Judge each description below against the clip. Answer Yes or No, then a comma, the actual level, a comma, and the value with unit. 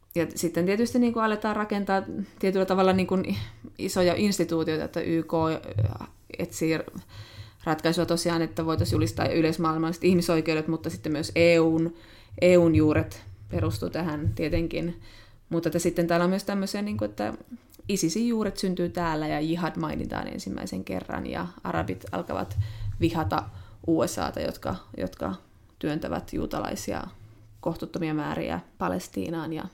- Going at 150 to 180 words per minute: No, average, 125 wpm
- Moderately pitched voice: Yes, medium, 165 Hz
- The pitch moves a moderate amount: No, wide, 8.2 semitones